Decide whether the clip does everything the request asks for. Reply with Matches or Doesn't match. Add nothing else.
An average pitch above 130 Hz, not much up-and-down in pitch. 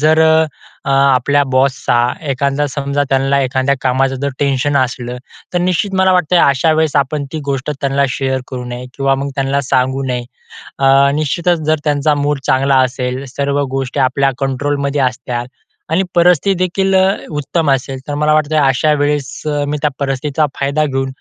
Matches